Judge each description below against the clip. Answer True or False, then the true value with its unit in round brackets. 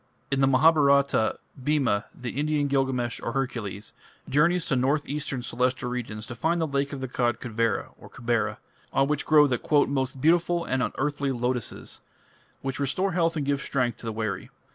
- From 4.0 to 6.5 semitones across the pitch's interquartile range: False (3.1 semitones)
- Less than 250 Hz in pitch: True (135 Hz)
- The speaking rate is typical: True (170 wpm)